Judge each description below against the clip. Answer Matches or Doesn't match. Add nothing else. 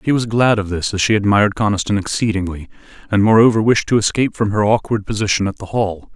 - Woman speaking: Doesn't match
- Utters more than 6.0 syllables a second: Matches